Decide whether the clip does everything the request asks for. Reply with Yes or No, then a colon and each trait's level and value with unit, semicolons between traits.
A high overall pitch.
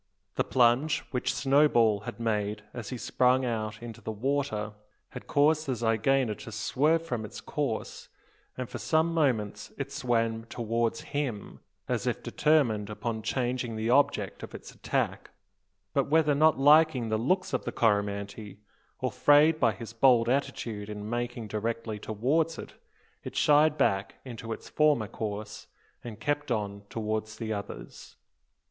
No: low, 120 Hz